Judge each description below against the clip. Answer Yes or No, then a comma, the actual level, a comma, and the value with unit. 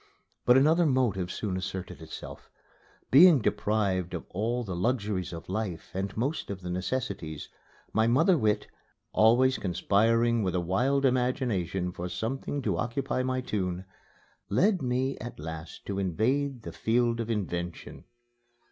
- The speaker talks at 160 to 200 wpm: No, average, 140 wpm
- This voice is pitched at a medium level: No, low, 110 Hz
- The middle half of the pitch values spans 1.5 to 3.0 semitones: No, wide, 5.6 semitones